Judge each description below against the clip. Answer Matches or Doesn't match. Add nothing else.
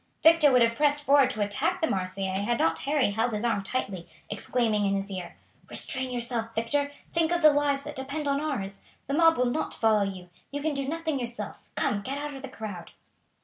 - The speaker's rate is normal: Doesn't match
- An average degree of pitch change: Doesn't match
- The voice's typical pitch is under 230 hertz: Doesn't match